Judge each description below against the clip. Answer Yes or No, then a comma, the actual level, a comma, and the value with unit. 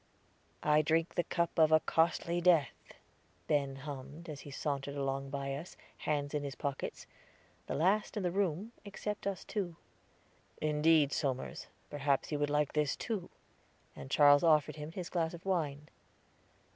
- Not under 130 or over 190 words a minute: Yes, average, 160 wpm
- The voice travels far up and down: No, average, 3.1 semitones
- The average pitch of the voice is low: No, medium, 150 Hz